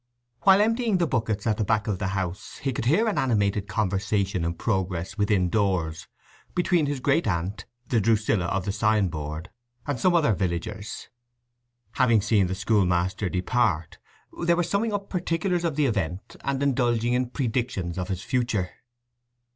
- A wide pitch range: Yes, wide, 6.2 semitones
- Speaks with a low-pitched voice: Yes, low, 110 Hz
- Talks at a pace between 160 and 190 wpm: Yes, average, 170 wpm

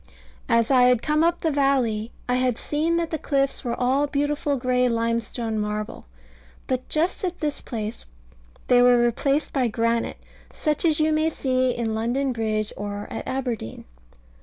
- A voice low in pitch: No, very high, 250 Hz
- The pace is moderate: Yes, average, 165 wpm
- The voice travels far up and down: No, average, 4.0 semitones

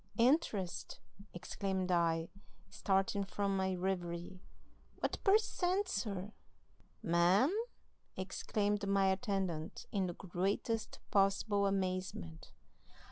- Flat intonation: Yes, narrow, 2.3 semitones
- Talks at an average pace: No, slow, 90 wpm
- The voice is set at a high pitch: Yes, high, 195 Hz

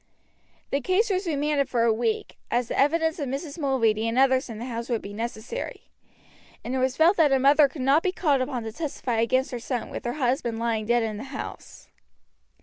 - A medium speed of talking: No, fast, 225 wpm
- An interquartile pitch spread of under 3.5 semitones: No, average, 3.8 semitones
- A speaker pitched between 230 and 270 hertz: Yes, very high, 260 Hz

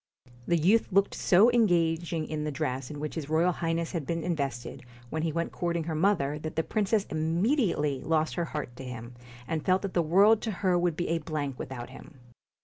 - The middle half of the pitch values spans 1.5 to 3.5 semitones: Yes, average, 2.9 semitones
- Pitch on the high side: No, medium, 165 Hz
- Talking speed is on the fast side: Yes, fast, 210 wpm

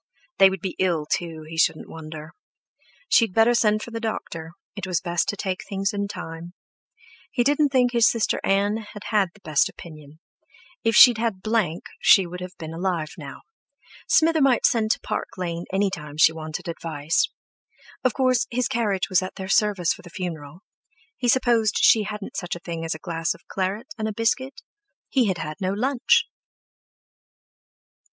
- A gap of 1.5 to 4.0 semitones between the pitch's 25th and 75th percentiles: No, average, 5.3 semitones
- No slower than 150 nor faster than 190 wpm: Yes, average, 180 wpm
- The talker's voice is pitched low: No, high, 195 Hz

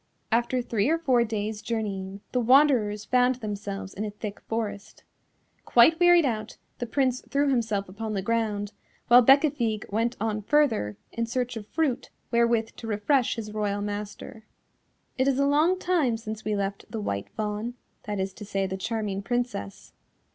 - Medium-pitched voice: No, high, 225 Hz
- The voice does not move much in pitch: No, average, 3.3 semitones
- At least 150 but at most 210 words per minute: Yes, average, 170 wpm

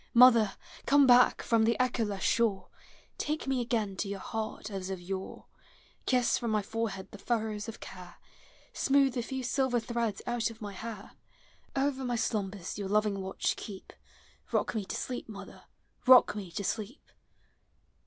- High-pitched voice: Yes, high, 220 Hz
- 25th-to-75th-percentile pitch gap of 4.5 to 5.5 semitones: No, average, 3.5 semitones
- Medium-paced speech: Yes, average, 165 wpm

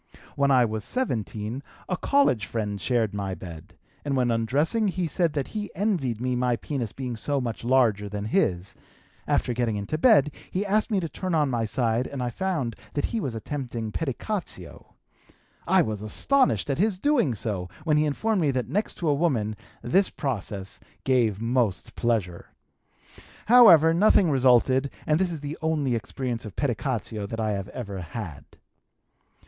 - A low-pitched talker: Yes, low, 130 Hz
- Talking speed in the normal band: Yes, average, 170 wpm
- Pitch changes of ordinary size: No, wide, 6.5 semitones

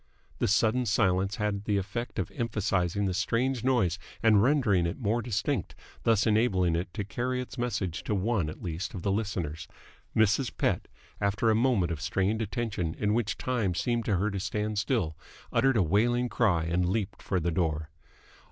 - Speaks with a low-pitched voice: Yes, low, 105 Hz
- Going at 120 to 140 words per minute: No, average, 180 wpm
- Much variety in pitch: No, average, 4.2 semitones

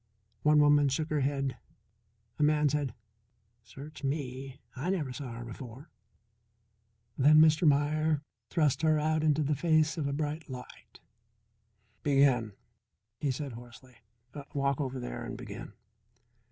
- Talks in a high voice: No, medium, 145 Hz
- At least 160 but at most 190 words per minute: No, slow, 135 wpm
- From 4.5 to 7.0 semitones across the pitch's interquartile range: No, average, 2.7 semitones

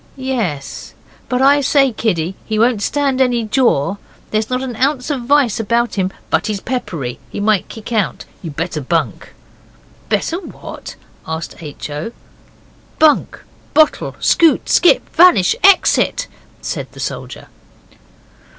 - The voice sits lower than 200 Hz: No, high, 235 Hz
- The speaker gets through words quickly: No, slow, 135 wpm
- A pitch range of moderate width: No, wide, 6.3 semitones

